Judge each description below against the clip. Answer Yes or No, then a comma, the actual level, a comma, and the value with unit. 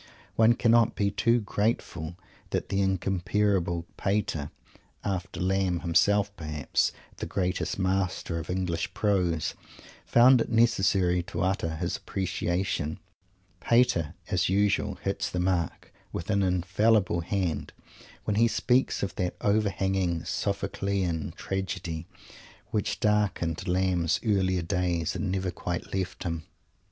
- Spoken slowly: Yes, slow, 120 wpm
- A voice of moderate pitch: No, very low, 95 Hz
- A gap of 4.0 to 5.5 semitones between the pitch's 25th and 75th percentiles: No, average, 2.7 semitones